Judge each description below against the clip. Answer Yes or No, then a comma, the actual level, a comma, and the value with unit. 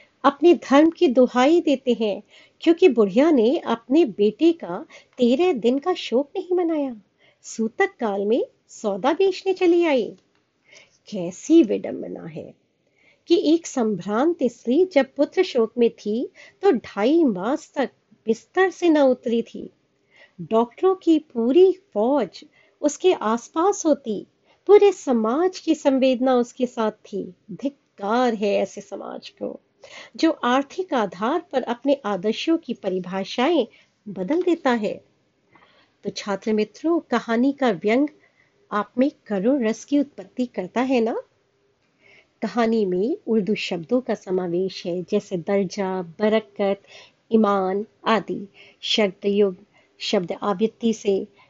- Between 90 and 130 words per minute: Yes, average, 125 wpm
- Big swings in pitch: Yes, wide, 7.1 semitones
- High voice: Yes, high, 240 Hz